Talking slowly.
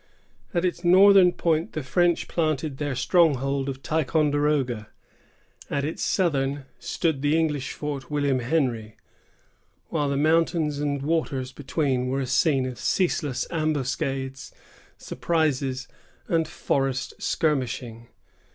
Yes: slow, 115 wpm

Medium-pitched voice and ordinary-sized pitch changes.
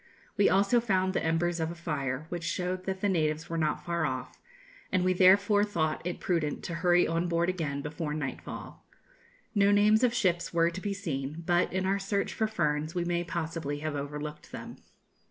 Yes: medium, 175 Hz; average, 3.3 semitones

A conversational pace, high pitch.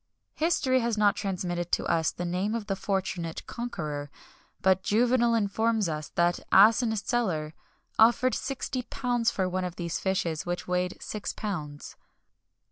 Yes: average, 145 wpm; high, 195 Hz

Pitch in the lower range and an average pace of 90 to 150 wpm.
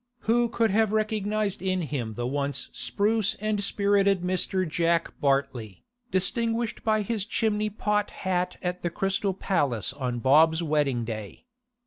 No: medium, 185 Hz; average, 140 wpm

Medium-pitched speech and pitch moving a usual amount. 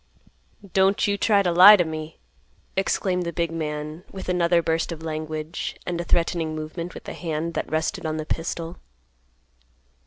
No: medium, 165 Hz; narrow, 2.2 semitones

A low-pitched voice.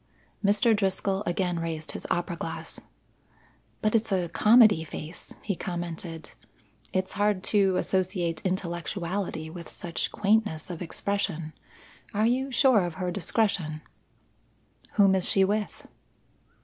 No: medium, 185 Hz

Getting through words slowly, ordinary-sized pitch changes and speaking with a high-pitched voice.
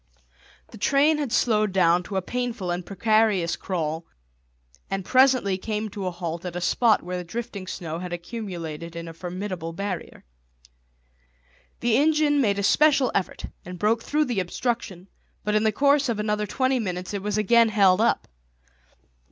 No: average, 170 wpm; average, 4.7 semitones; high, 205 Hz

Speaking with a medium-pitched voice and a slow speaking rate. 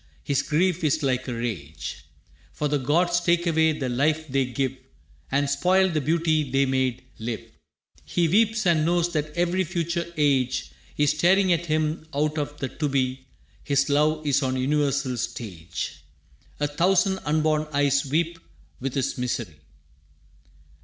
No: medium, 150 Hz; average, 155 wpm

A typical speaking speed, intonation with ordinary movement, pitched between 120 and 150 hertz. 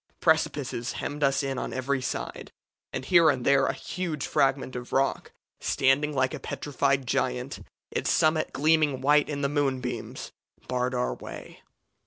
No: average, 155 wpm; narrow, 2.2 semitones; low, 135 Hz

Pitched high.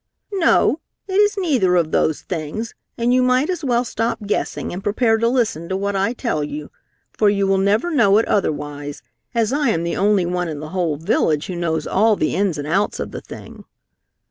Yes: high, 200 Hz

